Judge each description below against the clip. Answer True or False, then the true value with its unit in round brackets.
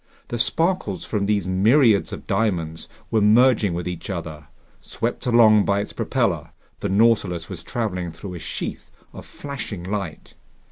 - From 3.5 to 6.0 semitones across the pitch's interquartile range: True (4.3 semitones)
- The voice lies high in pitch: False (100 Hz)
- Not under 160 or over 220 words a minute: False (150 wpm)